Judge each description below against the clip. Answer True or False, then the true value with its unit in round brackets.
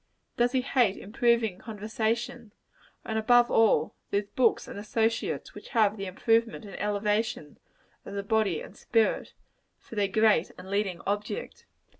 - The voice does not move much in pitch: True (2.3 semitones)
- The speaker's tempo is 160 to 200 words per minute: False (145 wpm)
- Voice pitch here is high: True (220 Hz)